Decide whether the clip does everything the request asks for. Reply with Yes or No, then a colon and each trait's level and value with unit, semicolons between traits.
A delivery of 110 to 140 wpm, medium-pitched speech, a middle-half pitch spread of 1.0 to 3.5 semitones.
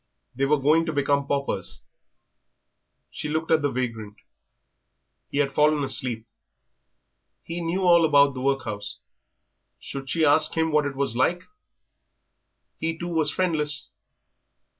Yes: slow, 135 wpm; medium, 145 Hz; average, 2.9 semitones